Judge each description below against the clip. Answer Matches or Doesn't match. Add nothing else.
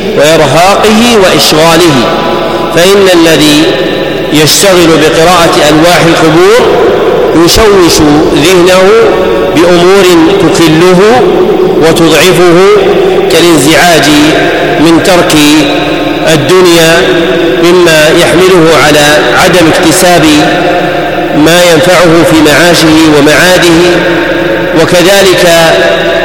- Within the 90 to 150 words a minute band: Doesn't match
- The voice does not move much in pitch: Matches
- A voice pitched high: Doesn't match